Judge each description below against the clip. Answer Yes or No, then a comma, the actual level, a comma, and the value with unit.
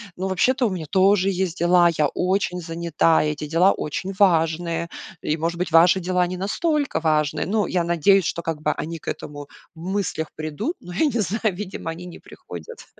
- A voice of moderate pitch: Yes, medium, 175 Hz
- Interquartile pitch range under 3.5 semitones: Yes, average, 2.9 semitones